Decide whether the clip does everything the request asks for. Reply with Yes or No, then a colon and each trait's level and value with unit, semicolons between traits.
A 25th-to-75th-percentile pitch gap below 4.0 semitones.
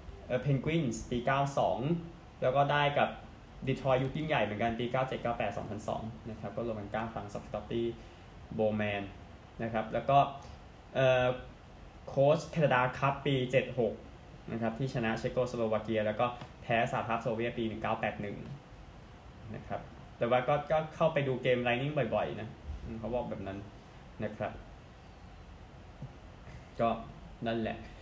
Yes: average, 3.5 semitones